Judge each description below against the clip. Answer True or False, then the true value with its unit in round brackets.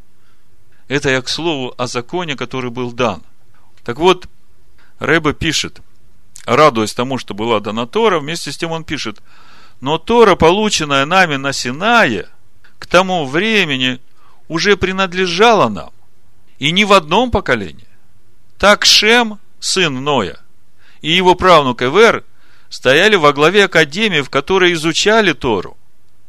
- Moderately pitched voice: True (145 Hz)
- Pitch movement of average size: False (7.7 semitones)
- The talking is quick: False (130 wpm)